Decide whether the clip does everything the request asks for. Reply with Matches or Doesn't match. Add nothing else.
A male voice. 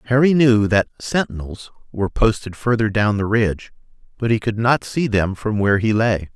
Matches